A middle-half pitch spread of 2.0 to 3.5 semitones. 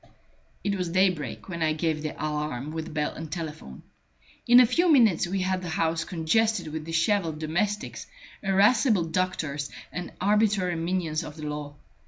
No: average, 4.1 semitones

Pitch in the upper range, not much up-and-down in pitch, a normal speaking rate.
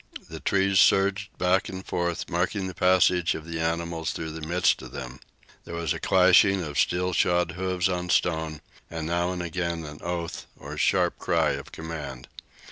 No: very low, 85 Hz; narrow, 2.1 semitones; average, 170 wpm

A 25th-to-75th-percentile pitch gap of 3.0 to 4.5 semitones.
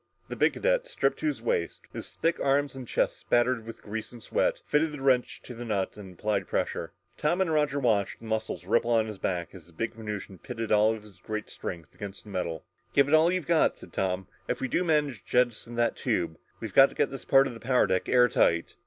No: average, 5.3 semitones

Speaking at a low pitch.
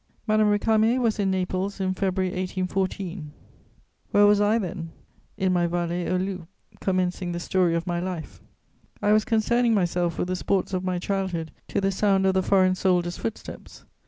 No: medium, 185 Hz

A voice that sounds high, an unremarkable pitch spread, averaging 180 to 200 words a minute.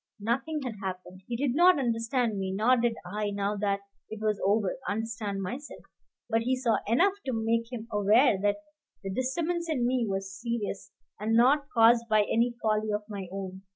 Yes: high, 225 Hz; average, 3.5 semitones; average, 185 wpm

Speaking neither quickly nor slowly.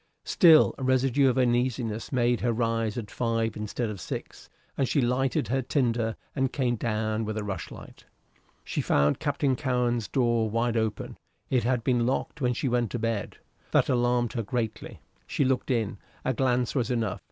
Yes: average, 175 wpm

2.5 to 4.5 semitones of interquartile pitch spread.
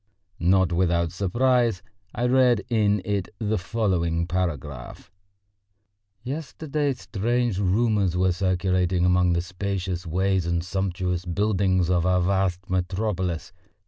Yes: average, 2.8 semitones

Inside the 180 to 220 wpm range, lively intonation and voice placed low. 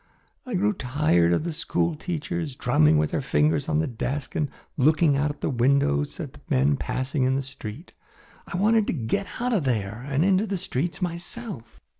No: average, 190 wpm; wide, 5.9 semitones; medium, 145 Hz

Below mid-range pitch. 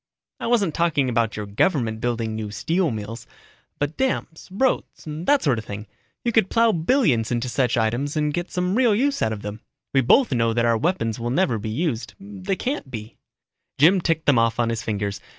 Yes: low, 130 Hz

